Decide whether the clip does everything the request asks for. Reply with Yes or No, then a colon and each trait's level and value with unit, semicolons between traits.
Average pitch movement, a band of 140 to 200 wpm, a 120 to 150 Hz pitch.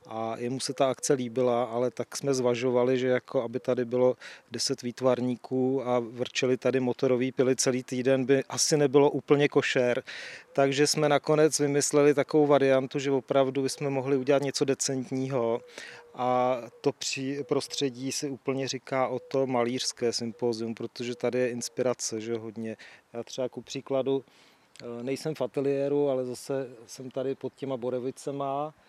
No: narrow, 2.0 semitones; average, 150 wpm; low, 130 Hz